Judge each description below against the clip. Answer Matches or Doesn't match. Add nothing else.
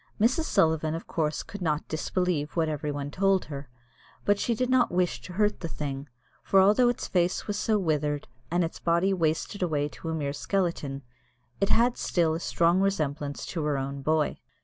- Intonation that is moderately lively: Matches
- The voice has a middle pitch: Matches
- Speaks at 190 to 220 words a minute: Matches